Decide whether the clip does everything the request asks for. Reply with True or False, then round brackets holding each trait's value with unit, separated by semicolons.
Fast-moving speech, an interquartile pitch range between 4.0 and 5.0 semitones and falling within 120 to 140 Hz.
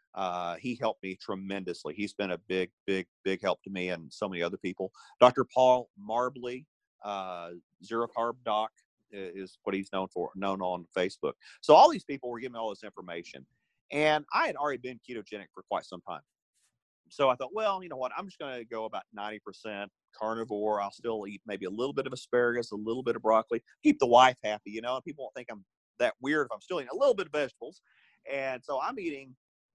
False (220 wpm; 4.6 semitones; 110 Hz)